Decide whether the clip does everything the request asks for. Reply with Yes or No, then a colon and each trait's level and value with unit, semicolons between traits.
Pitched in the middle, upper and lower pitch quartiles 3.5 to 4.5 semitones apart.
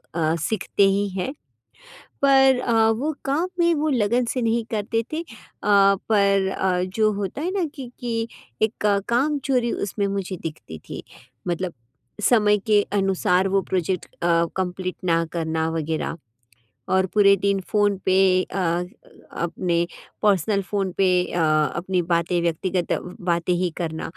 No: high, 195 Hz; average, 4.1 semitones